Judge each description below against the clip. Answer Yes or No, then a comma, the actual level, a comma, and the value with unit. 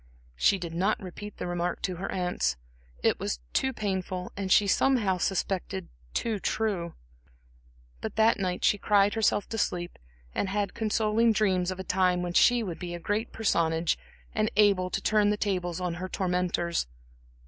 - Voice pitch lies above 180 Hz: Yes, high, 190 Hz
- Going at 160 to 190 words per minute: Yes, average, 170 wpm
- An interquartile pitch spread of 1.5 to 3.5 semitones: Yes, average, 2.8 semitones